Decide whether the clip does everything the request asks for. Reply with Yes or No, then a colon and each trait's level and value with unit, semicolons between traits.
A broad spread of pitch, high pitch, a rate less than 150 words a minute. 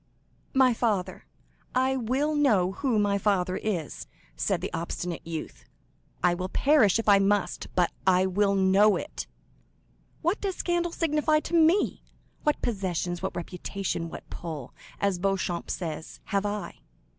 Yes: wide, 6.5 semitones; high, 200 Hz; average, 140 wpm